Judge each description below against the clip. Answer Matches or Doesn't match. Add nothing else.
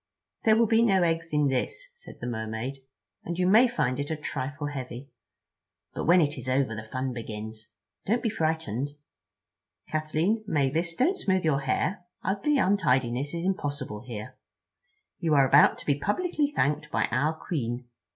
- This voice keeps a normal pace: Matches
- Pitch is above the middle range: Doesn't match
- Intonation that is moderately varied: Doesn't match